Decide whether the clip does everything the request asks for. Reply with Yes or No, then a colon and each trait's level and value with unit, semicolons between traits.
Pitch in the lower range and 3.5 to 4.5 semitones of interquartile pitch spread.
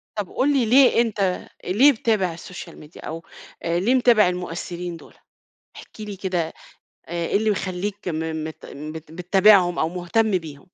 No: medium, 180 Hz; average, 4.1 semitones